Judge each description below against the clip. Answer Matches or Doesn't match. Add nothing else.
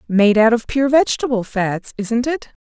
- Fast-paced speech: Doesn't match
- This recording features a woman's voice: Matches